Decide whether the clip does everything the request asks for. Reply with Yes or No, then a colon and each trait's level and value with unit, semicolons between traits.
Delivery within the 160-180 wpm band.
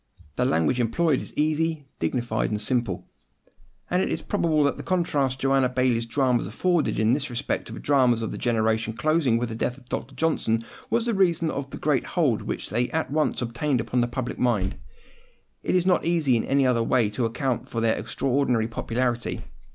No: average, 200 wpm